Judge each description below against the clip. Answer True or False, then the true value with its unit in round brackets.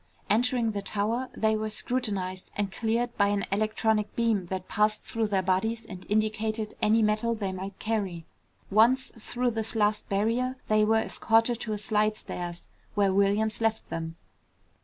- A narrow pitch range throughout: True (2.0 semitones)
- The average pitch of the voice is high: True (215 Hz)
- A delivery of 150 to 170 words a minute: True (160 wpm)